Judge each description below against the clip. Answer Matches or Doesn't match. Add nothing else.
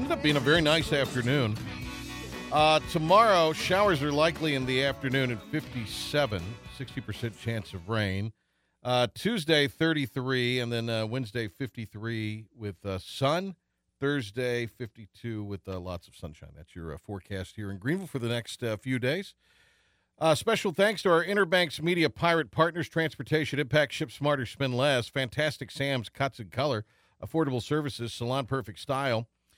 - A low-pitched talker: Matches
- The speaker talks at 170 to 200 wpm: Doesn't match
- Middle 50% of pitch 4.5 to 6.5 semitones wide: Matches